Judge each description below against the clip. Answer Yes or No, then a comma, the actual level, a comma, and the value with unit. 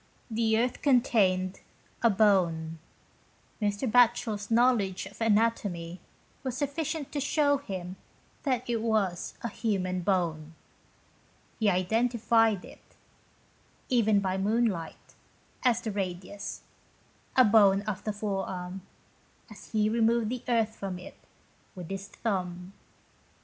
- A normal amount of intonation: Yes, average, 3.9 semitones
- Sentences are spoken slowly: Yes, slow, 120 wpm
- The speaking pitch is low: No, high, 210 Hz